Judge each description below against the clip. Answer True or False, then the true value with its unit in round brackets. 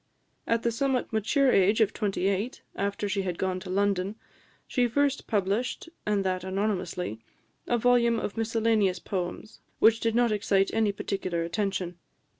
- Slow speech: False (155 wpm)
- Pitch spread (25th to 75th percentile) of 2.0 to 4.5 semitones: True (3.2 semitones)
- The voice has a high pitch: True (205 Hz)